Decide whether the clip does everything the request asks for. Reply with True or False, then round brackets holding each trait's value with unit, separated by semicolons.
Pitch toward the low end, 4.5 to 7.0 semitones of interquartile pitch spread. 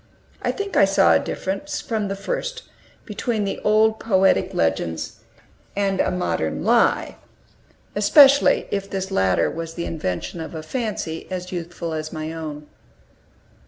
False (190 Hz; 4.9 semitones)